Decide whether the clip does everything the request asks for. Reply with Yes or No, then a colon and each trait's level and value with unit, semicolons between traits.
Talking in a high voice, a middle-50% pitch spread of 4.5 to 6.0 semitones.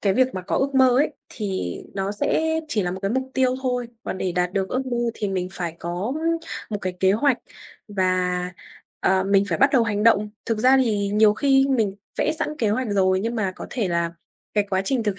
Yes: high, 210 Hz; average, 5.3 semitones